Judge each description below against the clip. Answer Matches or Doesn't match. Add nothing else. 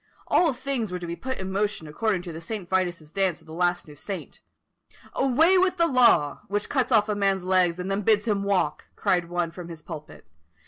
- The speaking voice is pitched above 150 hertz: Matches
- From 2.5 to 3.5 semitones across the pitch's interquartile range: Doesn't match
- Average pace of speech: Doesn't match